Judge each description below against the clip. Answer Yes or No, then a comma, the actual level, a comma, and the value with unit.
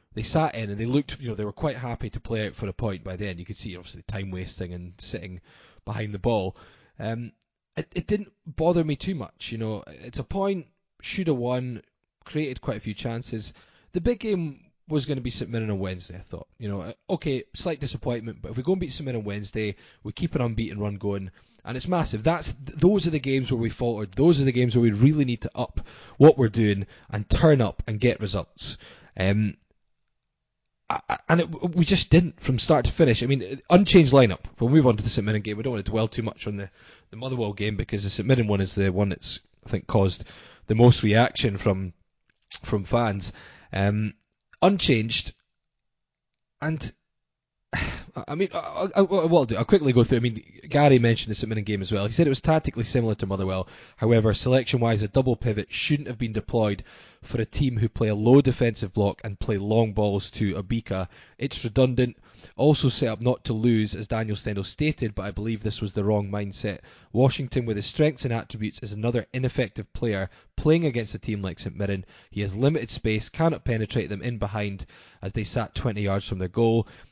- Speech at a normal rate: No, fast, 215 wpm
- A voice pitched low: Yes, low, 115 Hz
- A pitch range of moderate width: Yes, average, 4.4 semitones